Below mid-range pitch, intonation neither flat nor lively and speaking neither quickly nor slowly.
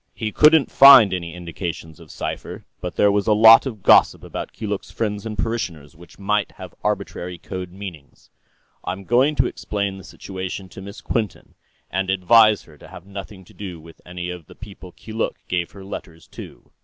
Yes: very low, 95 Hz; average, 3.3 semitones; average, 185 wpm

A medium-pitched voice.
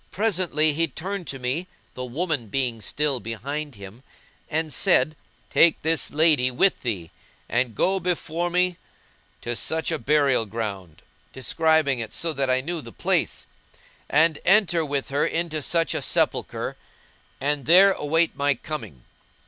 Yes: medium, 150 Hz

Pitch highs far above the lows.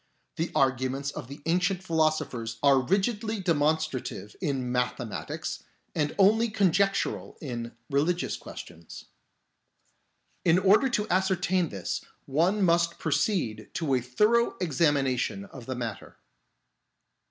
Yes: wide, 6.5 semitones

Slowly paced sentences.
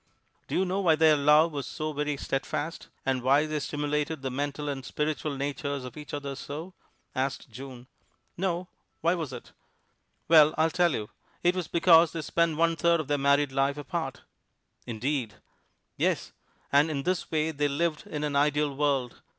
No: average, 175 wpm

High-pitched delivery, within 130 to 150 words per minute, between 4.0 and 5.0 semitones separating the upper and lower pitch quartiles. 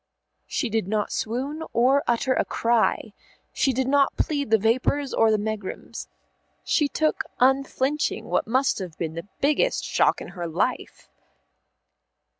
Yes: high, 245 Hz; average, 145 wpm; average, 4.3 semitones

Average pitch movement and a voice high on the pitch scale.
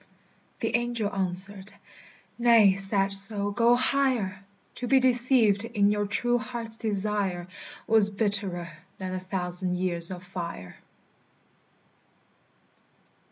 Yes: average, 3.7 semitones; high, 200 Hz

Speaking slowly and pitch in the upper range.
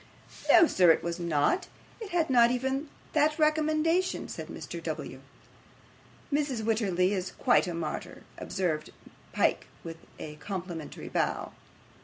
Yes: slow, 130 wpm; high, 225 Hz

